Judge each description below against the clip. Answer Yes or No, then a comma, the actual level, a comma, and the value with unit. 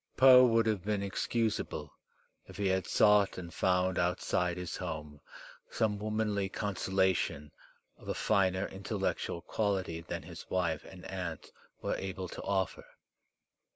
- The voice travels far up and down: No, narrow, 2.5 semitones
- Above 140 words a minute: No, slow, 135 wpm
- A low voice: Yes, very low, 95 Hz